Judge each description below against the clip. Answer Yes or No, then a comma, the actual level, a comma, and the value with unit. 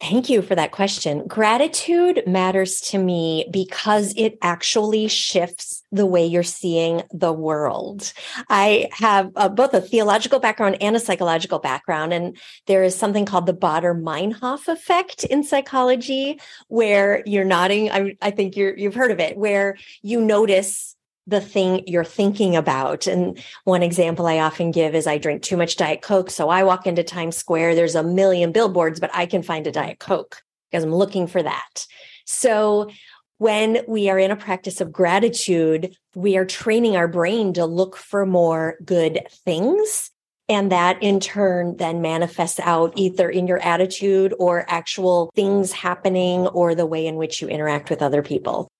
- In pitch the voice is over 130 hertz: Yes, high, 190 Hz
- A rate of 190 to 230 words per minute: No, average, 170 wpm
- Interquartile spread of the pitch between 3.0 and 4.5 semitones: Yes, average, 3.3 semitones